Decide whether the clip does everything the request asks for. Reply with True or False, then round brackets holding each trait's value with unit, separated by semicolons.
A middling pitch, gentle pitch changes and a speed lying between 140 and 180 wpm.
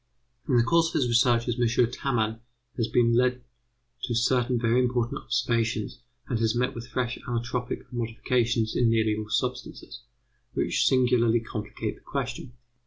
False (120 Hz; 1.4 semitones; 150 wpm)